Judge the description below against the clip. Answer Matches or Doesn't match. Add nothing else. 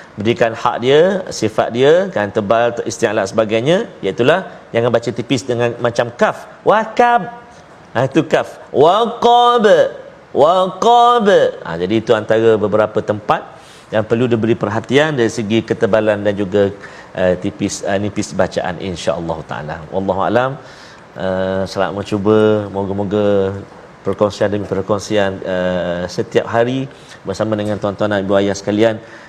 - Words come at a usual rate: Doesn't match